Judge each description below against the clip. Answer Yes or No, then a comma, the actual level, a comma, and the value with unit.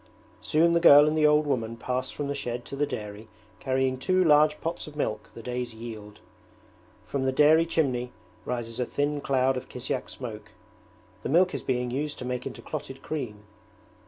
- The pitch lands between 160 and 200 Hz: No, low, 130 Hz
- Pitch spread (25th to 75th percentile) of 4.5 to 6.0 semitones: No, average, 3.6 semitones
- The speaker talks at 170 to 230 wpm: Yes, average, 190 wpm